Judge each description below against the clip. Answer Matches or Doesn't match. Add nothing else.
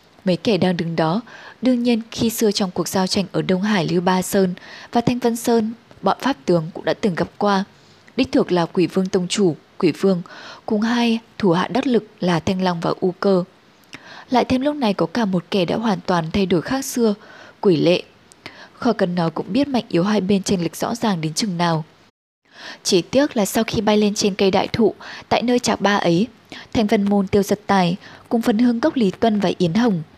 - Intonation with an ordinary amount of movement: Matches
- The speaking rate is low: Doesn't match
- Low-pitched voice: Doesn't match